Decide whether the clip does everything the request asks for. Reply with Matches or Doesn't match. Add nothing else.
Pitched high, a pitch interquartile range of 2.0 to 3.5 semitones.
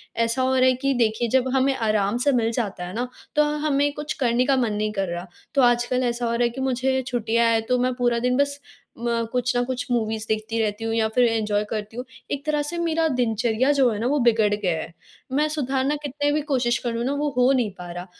Matches